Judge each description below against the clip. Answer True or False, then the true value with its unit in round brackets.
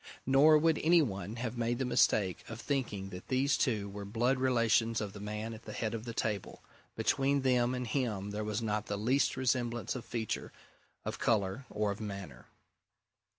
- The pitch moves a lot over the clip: False (3.6 semitones)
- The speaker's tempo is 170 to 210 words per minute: True (190 wpm)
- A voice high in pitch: False (115 Hz)